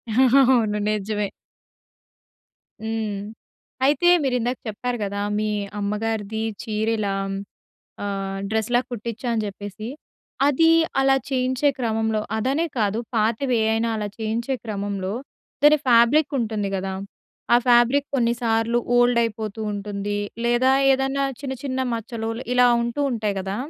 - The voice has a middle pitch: No, high, 225 Hz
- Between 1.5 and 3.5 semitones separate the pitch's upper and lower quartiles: Yes, average, 3.0 semitones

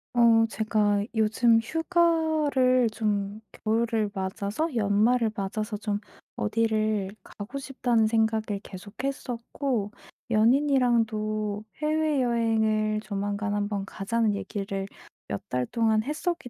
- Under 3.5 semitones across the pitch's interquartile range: Yes, average, 2.9 semitones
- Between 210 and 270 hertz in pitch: Yes, high, 220 Hz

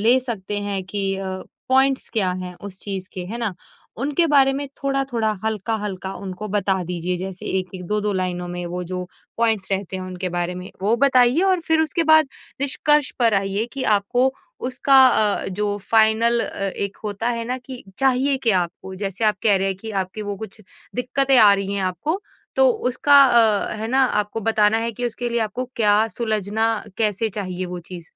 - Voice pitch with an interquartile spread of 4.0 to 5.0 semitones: Yes, average, 4.6 semitones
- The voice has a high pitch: Yes, high, 210 Hz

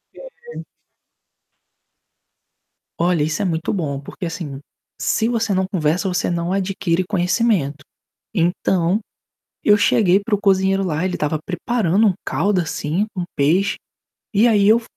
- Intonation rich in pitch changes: No, average, 3.7 semitones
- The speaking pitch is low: No, medium, 185 Hz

